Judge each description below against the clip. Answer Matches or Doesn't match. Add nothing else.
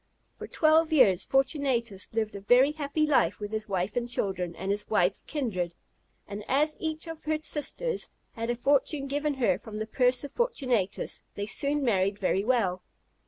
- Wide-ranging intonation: Matches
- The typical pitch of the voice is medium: Doesn't match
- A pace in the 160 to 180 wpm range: Matches